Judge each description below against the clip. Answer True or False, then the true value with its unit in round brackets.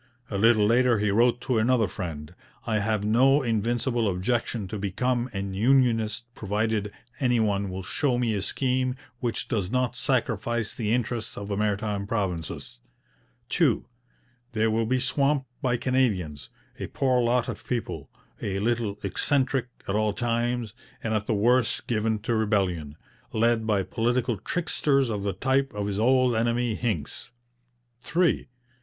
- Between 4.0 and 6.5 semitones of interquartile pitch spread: False (3.3 semitones)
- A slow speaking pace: False (150 wpm)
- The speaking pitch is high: False (115 Hz)